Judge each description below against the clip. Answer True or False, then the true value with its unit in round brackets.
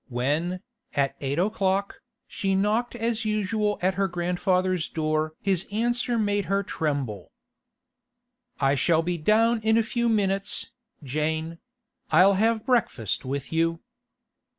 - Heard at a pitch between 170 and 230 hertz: True (185 Hz)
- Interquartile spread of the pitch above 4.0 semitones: True (5.3 semitones)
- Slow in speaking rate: True (130 wpm)